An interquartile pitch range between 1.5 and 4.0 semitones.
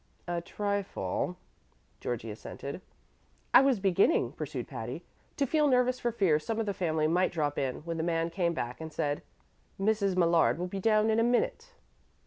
No: wide, 5.4 semitones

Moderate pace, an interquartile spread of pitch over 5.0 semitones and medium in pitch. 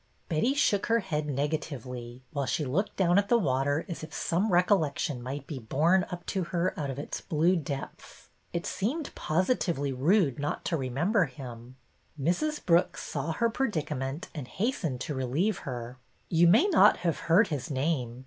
Yes: average, 180 wpm; wide, 5.6 semitones; medium, 155 Hz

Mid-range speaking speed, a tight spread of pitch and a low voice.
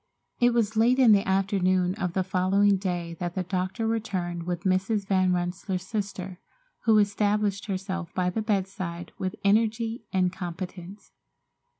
No: average, 150 wpm; narrow, 2.3 semitones; high, 190 Hz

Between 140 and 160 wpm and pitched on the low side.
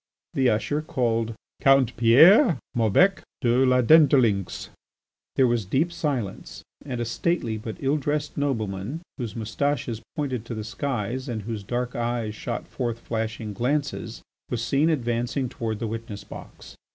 Yes: average, 145 wpm; low, 120 Hz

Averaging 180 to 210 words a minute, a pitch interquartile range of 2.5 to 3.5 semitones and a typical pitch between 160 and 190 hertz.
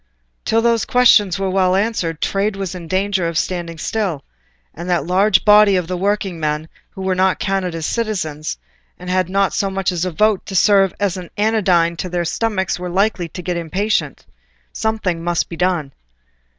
Yes: average, 190 wpm; average, 2.8 semitones; medium, 185 Hz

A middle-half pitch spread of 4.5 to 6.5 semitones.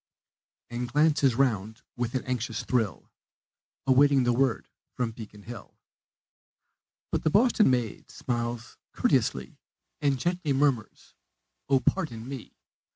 No: average, 3.3 semitones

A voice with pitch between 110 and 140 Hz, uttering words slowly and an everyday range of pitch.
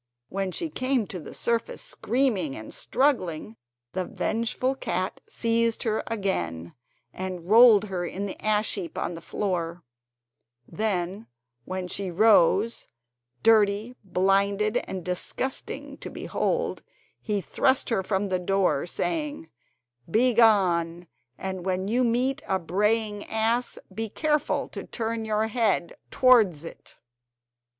No: high, 205 Hz; slow, 125 wpm; average, 3.9 semitones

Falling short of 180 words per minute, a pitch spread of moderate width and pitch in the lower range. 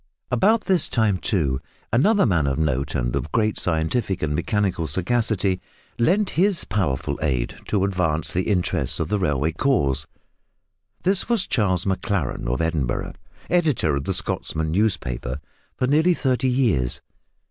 No: average, 145 wpm; wide, 8.4 semitones; very low, 95 Hz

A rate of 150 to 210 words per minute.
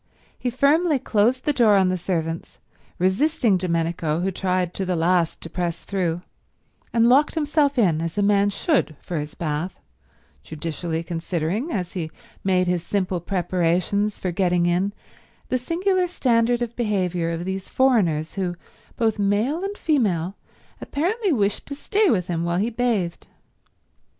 Yes: average, 155 wpm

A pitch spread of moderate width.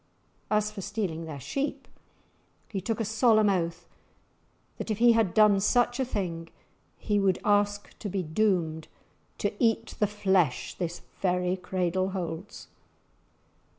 Yes: average, 3.3 semitones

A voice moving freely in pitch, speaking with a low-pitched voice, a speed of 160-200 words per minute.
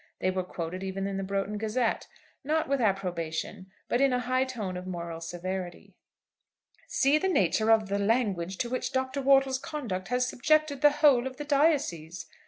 No: wide, 6.2 semitones; high, 220 Hz; average, 180 wpm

